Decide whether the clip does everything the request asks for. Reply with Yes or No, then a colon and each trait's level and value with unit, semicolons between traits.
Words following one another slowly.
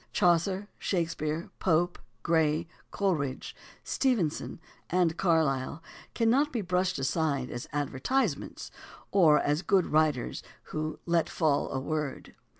Yes: slow, 115 wpm